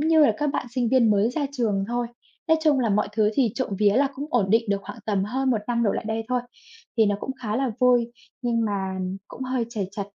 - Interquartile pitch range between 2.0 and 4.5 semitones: Yes, average, 3.7 semitones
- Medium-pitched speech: No, high, 235 Hz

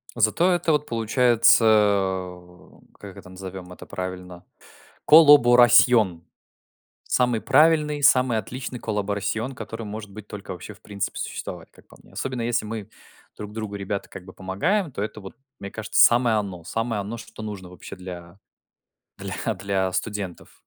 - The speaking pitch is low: Yes, low, 105 Hz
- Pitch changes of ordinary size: Yes, average, 4.1 semitones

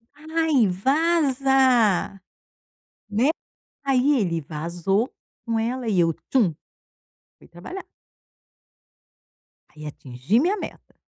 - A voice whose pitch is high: Yes, high, 230 Hz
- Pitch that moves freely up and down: Yes, wide, 7.7 semitones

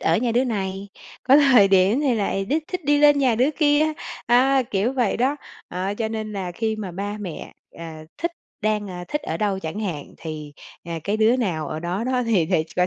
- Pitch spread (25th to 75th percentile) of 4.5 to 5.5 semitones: Yes, average, 5.2 semitones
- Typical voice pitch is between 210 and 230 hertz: Yes, high, 215 Hz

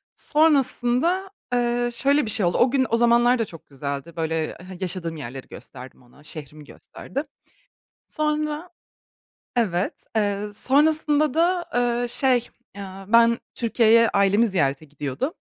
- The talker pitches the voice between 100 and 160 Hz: No, high, 230 Hz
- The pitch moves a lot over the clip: Yes, wide, 7.8 semitones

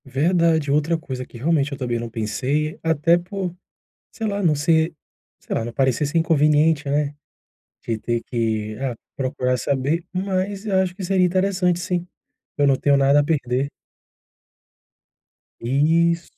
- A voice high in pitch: No, medium, 150 Hz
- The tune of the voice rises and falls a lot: No, average, 4.5 semitones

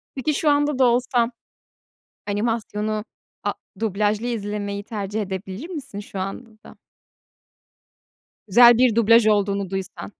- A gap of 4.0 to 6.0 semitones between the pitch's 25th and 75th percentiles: No, average, 3.1 semitones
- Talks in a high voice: Yes, high, 215 Hz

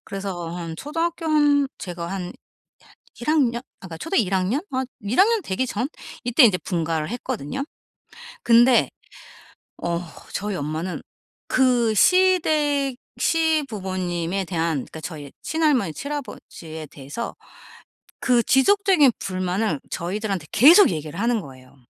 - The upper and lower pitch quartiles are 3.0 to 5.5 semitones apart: No, wide, 8.7 semitones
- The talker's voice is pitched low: No, high, 215 Hz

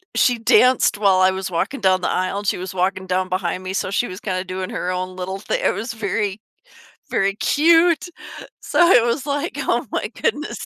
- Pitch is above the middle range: Yes, high, 195 Hz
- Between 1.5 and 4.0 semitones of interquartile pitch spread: No, average, 4.7 semitones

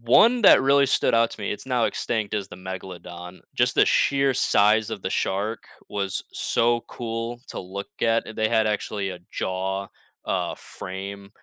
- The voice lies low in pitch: Yes, low, 105 Hz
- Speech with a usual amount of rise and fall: Yes, average, 3.4 semitones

